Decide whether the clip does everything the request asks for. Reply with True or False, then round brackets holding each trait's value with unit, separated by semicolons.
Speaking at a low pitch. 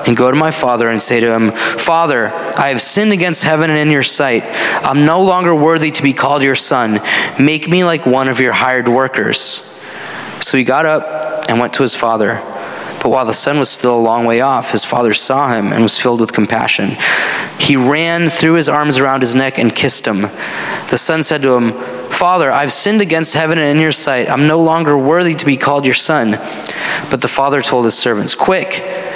False (145 Hz)